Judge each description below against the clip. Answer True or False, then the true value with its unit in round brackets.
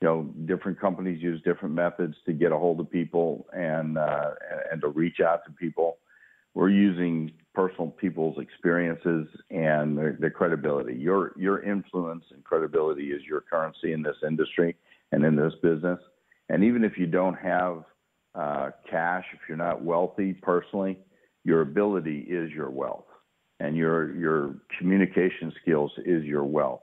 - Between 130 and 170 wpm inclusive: True (160 wpm)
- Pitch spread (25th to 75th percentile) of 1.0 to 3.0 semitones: True (2.6 semitones)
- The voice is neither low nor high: False (85 Hz)